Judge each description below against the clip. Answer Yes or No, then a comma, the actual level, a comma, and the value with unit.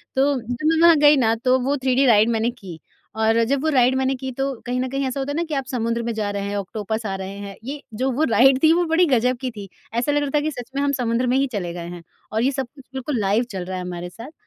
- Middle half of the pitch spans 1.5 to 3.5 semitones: No, average, 3.9 semitones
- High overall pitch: Yes, very high, 250 Hz